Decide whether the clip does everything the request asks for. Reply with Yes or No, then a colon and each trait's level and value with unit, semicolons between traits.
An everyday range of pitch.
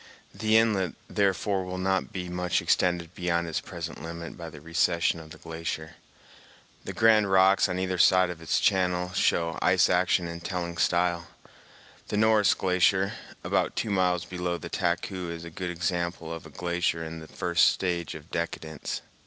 No: narrow, 1.8 semitones